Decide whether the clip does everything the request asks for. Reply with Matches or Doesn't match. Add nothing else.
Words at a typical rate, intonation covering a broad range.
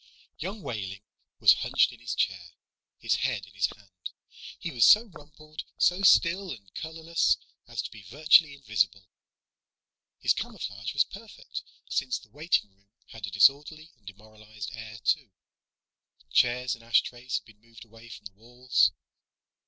Matches